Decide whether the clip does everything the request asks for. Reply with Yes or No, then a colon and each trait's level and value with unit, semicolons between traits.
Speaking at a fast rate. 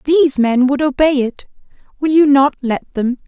No: average, 185 wpm